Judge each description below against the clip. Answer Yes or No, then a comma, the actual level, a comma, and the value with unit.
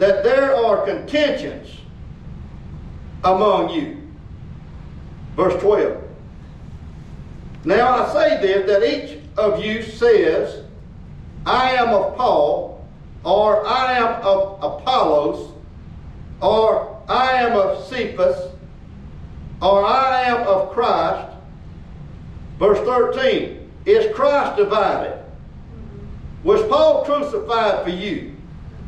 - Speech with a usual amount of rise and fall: No, wide, 7.6 semitones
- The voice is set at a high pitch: Yes, high, 245 Hz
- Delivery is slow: Yes, slow, 95 wpm